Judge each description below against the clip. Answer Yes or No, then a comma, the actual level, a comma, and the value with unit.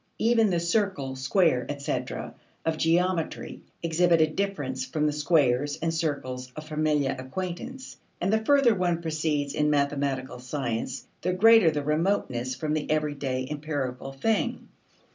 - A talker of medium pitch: Yes, medium, 155 Hz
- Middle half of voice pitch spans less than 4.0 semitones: No, average, 4.3 semitones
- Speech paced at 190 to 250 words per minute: No, average, 140 wpm